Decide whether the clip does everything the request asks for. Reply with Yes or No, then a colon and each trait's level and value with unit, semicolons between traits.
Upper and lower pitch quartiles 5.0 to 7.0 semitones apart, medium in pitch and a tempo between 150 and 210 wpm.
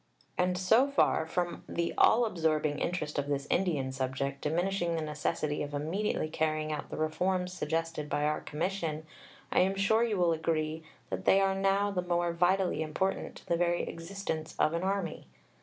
No: average, 3.6 semitones; medium, 170 Hz; average, 175 wpm